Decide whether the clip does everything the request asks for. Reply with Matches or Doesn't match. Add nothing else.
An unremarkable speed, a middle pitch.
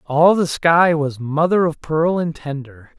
Matches